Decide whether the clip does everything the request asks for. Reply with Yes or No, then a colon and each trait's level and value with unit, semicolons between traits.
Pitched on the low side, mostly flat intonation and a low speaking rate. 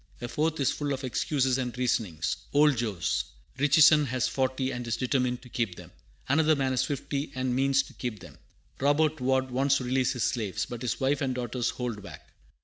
No: low, 130 Hz; narrow, 2.2 semitones; average, 200 wpm